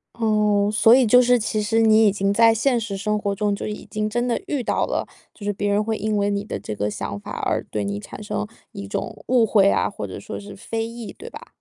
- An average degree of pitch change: No, narrow, 2.0 semitones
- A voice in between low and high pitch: No, high, 210 Hz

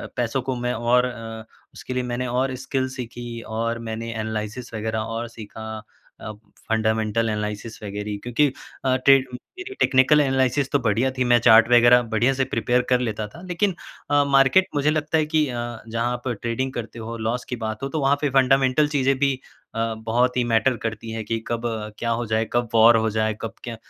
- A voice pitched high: No, low, 120 Hz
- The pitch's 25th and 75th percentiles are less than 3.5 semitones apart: Yes, average, 2.8 semitones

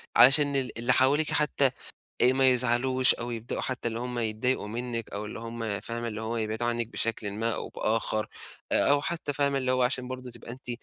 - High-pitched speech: No, low, 120 Hz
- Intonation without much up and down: Yes, narrow, 2.3 semitones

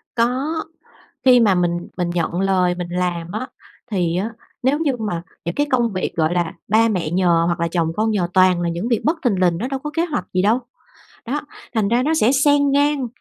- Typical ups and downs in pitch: No, wide, 6.5 semitones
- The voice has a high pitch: Yes, high, 205 Hz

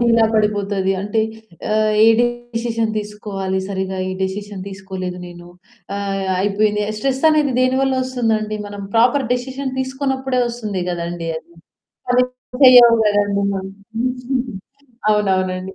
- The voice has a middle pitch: No, high, 210 Hz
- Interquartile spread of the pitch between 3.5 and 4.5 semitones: Yes, average, 4.1 semitones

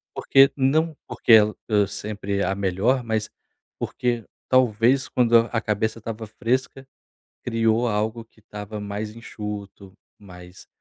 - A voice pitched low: Yes, low, 110 Hz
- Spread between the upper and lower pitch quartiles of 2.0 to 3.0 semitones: Yes, narrow, 2.5 semitones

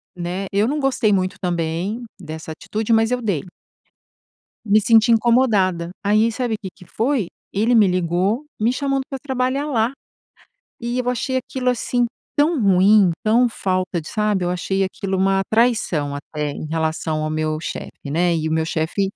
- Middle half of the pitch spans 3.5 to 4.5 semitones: No, wide, 5.5 semitones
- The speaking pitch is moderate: No, high, 200 Hz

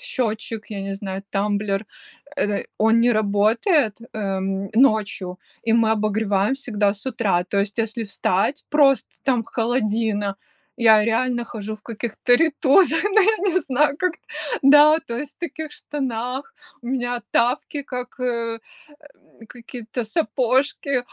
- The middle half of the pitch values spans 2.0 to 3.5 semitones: No, average, 4.1 semitones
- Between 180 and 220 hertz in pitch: No, high, 230 Hz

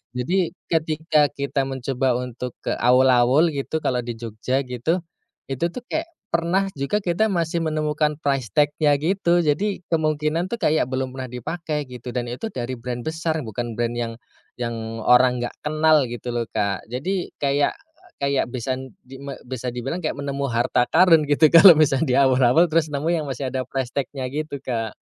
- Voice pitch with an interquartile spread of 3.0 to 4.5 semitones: Yes, average, 4.1 semitones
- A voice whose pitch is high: No, medium, 140 Hz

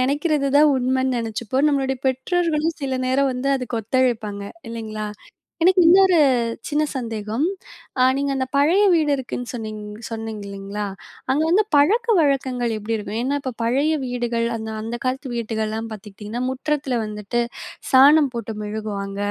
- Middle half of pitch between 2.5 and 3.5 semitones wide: No, average, 4.3 semitones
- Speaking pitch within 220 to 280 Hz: Yes, very high, 255 Hz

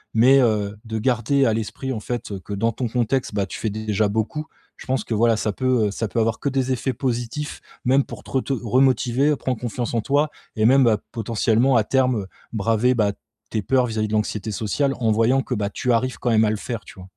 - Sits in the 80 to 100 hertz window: No, low, 115 Hz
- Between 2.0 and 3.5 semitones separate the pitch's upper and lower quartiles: Yes, average, 3.1 semitones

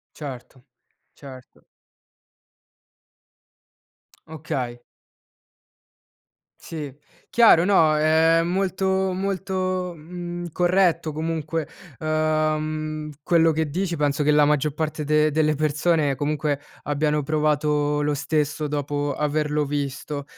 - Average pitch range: No, narrow, 2.0 semitones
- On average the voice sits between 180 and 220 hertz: No, medium, 155 Hz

